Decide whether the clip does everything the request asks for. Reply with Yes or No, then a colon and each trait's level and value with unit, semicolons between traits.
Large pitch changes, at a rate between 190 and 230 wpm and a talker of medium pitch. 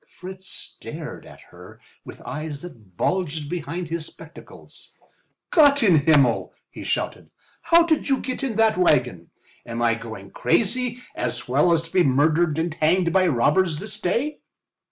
No: wide, 5.7 semitones; average, 155 wpm; medium, 170 Hz